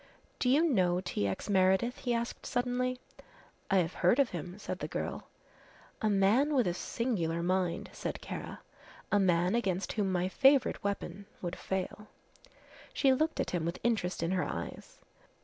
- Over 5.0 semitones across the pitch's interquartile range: Yes, wide, 5.5 semitones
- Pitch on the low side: No, high, 195 Hz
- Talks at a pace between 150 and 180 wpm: Yes, average, 165 wpm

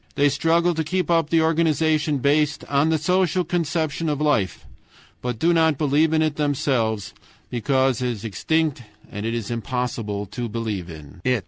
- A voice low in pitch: No, medium, 145 Hz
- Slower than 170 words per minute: No, average, 175 wpm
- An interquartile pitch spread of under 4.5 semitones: No, average, 5.3 semitones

